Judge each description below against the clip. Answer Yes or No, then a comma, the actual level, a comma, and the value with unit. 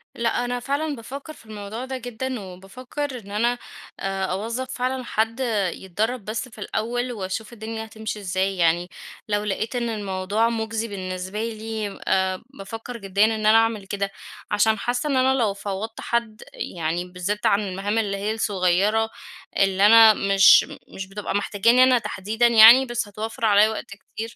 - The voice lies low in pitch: No, high, 220 Hz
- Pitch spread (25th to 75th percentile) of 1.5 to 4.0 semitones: Yes, average, 3.1 semitones